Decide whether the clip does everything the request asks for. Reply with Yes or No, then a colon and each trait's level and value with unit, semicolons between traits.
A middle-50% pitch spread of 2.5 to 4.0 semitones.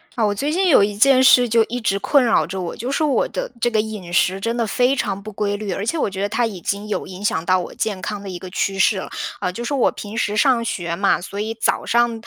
Yes: average, 3.5 semitones